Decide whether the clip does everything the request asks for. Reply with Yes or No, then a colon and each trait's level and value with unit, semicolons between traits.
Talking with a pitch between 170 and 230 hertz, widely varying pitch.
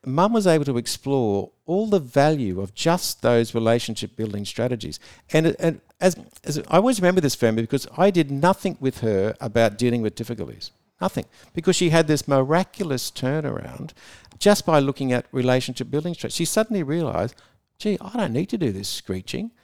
No: medium, 140 Hz; wide, 6.9 semitones